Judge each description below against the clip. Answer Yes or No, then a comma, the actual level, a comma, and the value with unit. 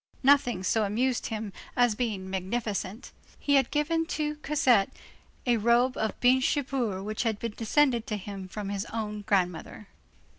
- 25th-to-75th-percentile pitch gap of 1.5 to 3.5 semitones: No, average, 4.2 semitones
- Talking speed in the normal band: Yes, average, 150 wpm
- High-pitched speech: Yes, high, 225 Hz